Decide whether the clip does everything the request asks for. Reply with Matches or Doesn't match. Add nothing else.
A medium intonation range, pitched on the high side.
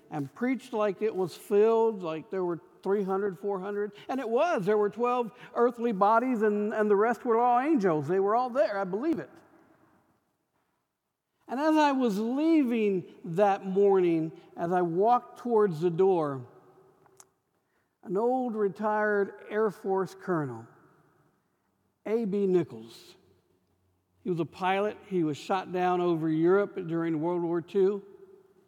Matches